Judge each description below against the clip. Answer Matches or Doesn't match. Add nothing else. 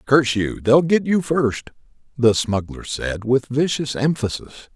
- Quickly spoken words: Doesn't match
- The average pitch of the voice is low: Matches